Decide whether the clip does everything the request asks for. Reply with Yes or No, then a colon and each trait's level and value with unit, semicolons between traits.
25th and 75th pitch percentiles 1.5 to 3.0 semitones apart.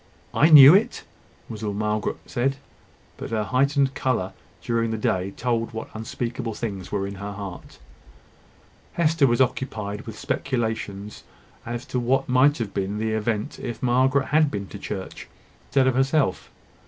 No: average, 4.1 semitones